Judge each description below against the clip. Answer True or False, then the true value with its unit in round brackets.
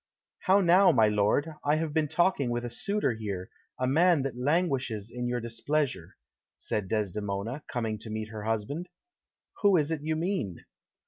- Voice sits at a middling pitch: False (125 Hz)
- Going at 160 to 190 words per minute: True (170 wpm)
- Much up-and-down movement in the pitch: True (6.6 semitones)